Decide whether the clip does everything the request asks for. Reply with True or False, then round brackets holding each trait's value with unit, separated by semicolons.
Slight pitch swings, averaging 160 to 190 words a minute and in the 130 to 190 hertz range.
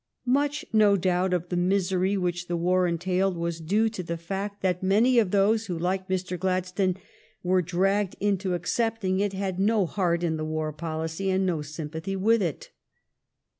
True (2.3 semitones; 175 wpm; 185 Hz)